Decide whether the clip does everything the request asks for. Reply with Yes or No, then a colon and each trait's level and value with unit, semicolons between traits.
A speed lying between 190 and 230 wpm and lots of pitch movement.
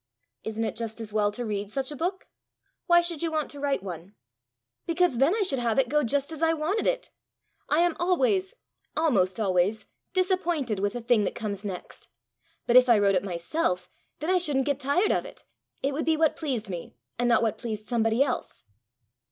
Yes: fast, 205 wpm; wide, 7.2 semitones